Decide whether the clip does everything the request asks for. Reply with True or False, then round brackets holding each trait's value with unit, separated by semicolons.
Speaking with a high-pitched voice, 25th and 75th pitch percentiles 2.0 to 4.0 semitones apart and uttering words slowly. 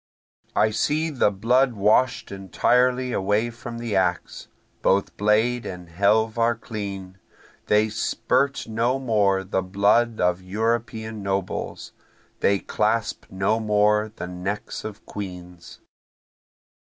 False (105 Hz; 3.1 semitones; 115 wpm)